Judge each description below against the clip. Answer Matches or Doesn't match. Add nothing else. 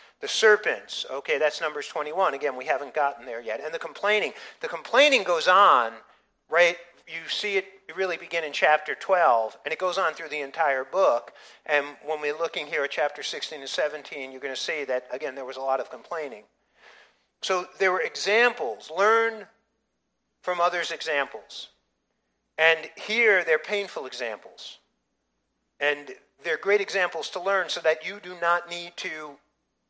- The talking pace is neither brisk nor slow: Matches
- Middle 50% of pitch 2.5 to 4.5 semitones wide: Doesn't match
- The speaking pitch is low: Doesn't match